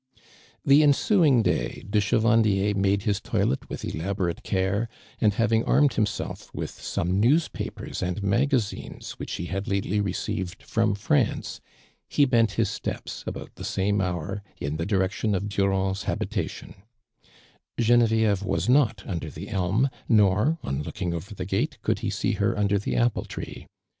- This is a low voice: Yes, low, 100 Hz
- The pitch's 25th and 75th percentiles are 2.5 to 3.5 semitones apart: Yes, average, 3.1 semitones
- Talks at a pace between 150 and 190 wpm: Yes, average, 155 wpm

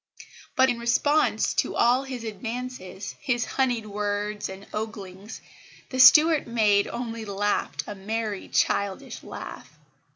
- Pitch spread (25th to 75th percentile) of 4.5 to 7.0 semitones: No, average, 3.5 semitones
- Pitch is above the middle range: Yes, high, 225 Hz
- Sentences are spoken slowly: Yes, slow, 125 wpm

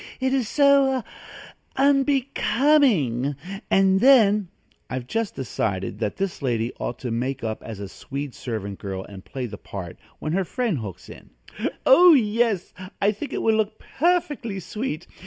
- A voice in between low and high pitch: No, high, 195 Hz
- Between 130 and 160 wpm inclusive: Yes, average, 155 wpm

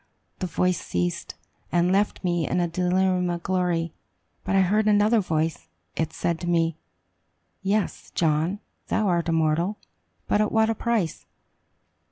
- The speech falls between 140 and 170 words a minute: Yes, average, 150 wpm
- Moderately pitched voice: Yes, medium, 180 Hz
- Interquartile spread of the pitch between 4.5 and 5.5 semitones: No, average, 3.3 semitones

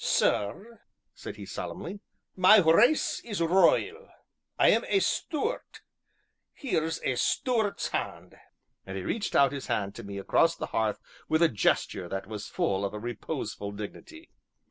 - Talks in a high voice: No, medium, 160 Hz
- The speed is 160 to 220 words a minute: No, average, 150 wpm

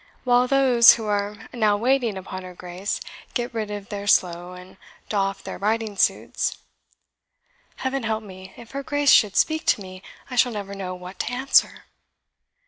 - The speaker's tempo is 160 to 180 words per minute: Yes, average, 170 wpm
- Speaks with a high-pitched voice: Yes, high, 210 Hz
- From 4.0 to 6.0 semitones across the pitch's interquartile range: Yes, average, 4.4 semitones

